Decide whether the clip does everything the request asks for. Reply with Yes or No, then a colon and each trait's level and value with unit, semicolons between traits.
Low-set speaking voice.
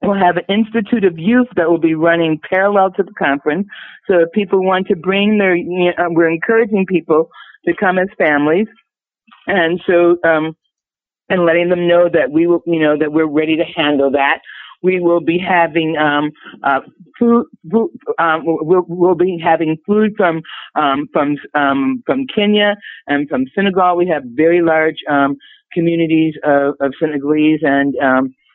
No: medium, 170 Hz